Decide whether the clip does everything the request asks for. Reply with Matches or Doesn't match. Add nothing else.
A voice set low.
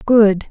Doesn't match